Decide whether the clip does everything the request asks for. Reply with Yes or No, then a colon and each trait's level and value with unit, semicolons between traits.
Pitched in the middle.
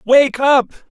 No: very high, 270 Hz